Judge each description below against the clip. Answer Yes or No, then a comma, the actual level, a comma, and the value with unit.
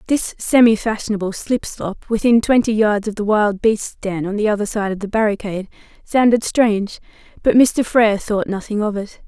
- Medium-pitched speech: No, high, 215 Hz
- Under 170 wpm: No, average, 190 wpm